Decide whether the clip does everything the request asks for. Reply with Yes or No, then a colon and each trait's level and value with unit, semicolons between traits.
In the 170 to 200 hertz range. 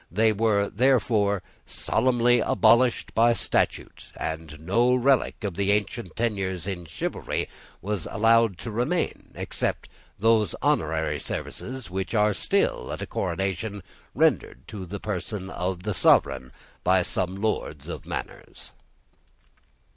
No: low, 105 Hz